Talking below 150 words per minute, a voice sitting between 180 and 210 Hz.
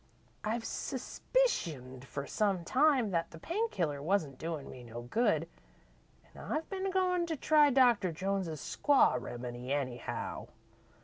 Yes: slow, 135 wpm; medium, 185 Hz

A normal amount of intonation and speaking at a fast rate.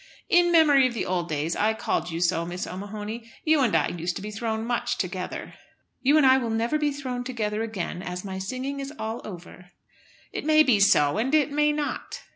No: wide, 6.5 semitones; fast, 215 wpm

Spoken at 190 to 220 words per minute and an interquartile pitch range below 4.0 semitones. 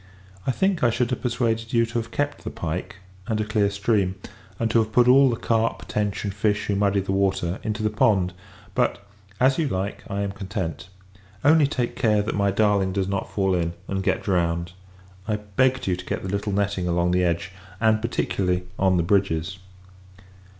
Yes: average, 200 wpm; average, 3.2 semitones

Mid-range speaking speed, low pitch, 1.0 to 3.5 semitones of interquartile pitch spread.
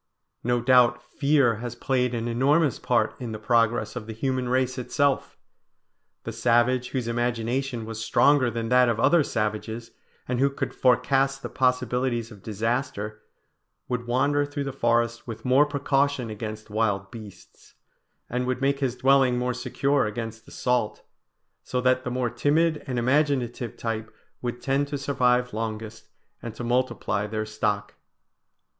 Yes: average, 150 wpm; low, 125 Hz; average, 2.7 semitones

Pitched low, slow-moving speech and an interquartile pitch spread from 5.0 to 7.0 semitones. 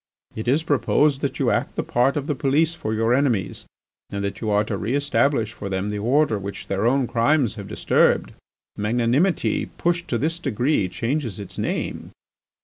No: low, 120 Hz; average, 185 wpm; wide, 5.5 semitones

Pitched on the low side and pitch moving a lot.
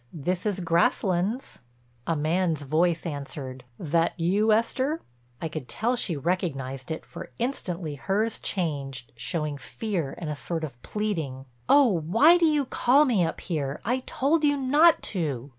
No: medium, 175 Hz; wide, 7.1 semitones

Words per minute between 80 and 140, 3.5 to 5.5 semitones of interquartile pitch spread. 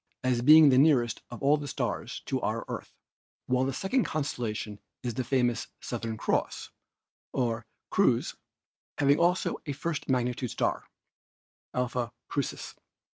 No: slow, 135 wpm; average, 3.1 semitones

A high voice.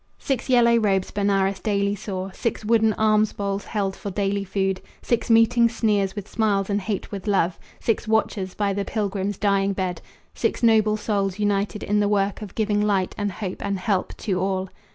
Yes: high, 205 Hz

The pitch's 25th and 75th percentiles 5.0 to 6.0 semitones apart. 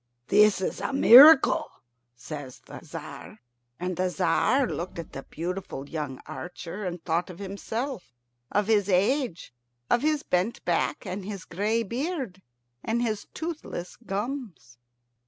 Yes: average, 5.3 semitones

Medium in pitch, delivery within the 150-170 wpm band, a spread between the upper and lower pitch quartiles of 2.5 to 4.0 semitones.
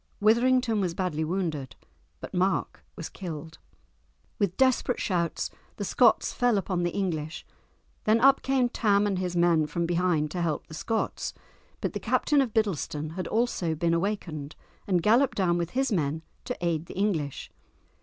No: medium, 180 Hz; average, 165 wpm; average, 4.8 semitones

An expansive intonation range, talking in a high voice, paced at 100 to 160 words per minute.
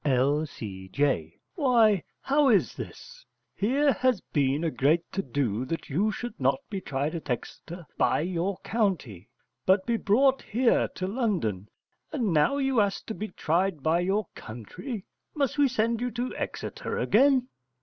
Yes: wide, 8.8 semitones; high, 195 Hz; average, 155 wpm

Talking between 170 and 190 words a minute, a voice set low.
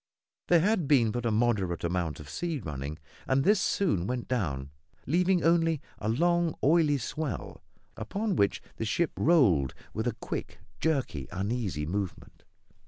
No: average, 150 wpm; low, 120 Hz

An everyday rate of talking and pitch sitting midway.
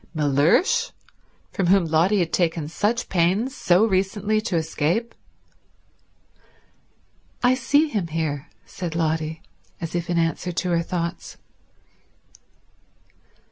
No: slow, 110 wpm; medium, 175 Hz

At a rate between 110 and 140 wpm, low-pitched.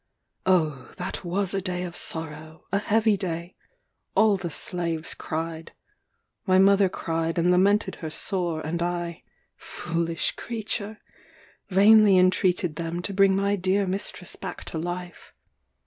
No: slow, 135 wpm; medium, 180 Hz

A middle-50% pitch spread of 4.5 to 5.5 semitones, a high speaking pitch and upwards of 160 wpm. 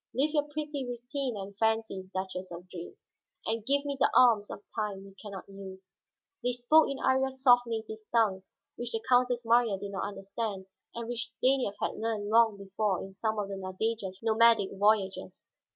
No: average, 3.8 semitones; high, 220 Hz; average, 185 wpm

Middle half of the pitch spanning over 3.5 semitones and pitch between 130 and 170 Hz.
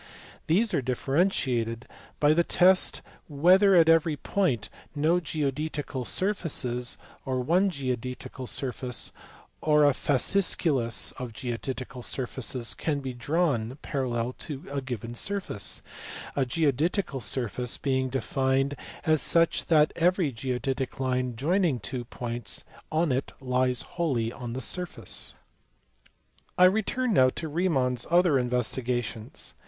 Yes: average, 4.7 semitones; low, 135 Hz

